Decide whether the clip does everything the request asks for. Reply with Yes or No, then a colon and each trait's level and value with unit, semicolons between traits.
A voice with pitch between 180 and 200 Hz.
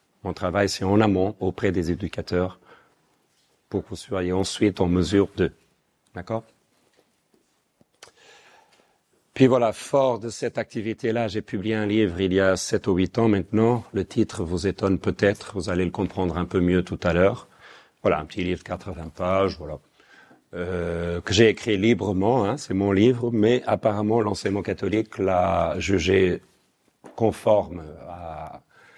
No: very low, 95 Hz